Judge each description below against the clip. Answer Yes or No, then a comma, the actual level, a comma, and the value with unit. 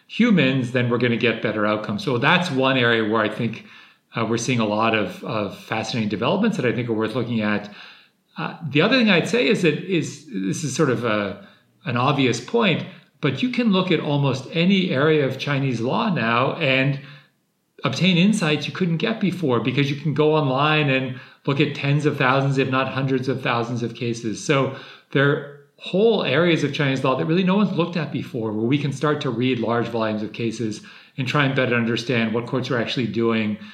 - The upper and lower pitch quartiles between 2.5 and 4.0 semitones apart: No, average, 4.9 semitones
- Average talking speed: No, fast, 215 wpm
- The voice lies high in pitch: No, low, 135 Hz